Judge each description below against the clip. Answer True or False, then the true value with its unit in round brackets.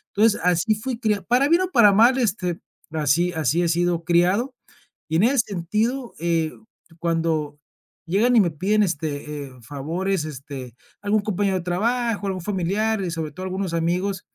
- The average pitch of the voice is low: False (185 Hz)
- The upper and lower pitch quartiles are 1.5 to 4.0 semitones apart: False (4.5 semitones)